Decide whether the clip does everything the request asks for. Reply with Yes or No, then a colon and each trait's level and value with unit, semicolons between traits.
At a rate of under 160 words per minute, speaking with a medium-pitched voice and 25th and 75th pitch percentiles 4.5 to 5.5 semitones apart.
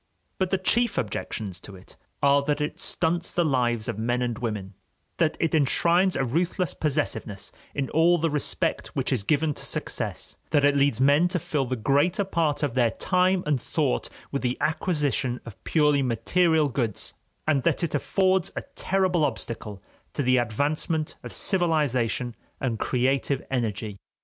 No: average, 165 wpm; medium, 145 Hz; average, 5.2 semitones